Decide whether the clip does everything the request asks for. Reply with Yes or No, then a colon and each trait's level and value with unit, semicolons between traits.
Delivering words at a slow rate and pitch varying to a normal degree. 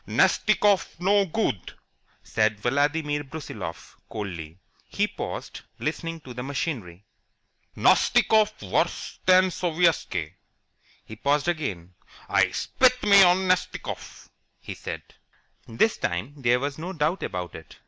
No: slow, 115 wpm; wide, 8.7 semitones